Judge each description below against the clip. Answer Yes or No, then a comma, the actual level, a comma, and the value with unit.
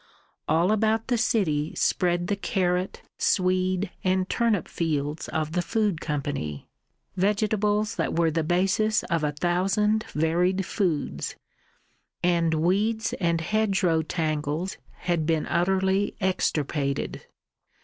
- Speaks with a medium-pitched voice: Yes, medium, 180 Hz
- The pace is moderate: No, slow, 115 wpm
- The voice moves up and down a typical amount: Yes, average, 3.9 semitones